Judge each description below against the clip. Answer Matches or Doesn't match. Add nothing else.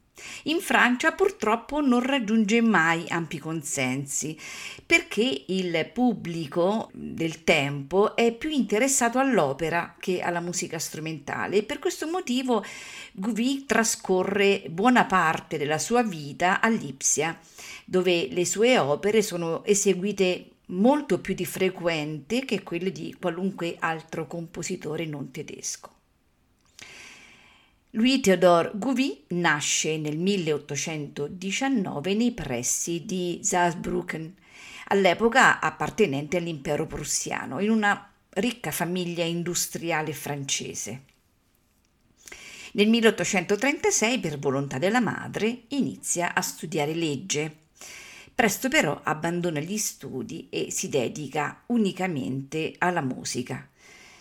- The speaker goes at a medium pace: Doesn't match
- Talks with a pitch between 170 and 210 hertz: Matches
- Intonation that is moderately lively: Doesn't match